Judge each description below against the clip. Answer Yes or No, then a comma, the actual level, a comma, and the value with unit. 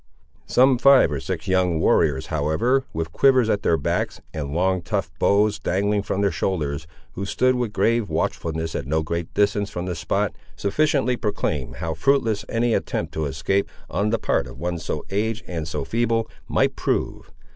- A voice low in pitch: Yes, very low, 95 Hz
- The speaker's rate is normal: Yes, average, 180 wpm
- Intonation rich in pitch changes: Yes, wide, 5.8 semitones